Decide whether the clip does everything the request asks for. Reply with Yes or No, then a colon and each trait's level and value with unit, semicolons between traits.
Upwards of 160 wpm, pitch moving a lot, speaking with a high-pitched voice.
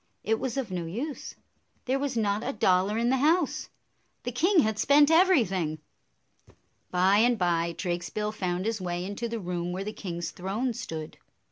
Yes: average, 170 wpm; wide, 5.7 semitones; high, 210 Hz